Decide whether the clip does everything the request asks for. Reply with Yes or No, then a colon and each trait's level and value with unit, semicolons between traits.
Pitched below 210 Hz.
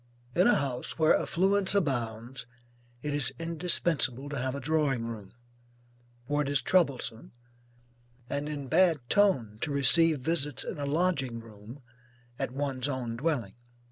Yes: medium, 140 Hz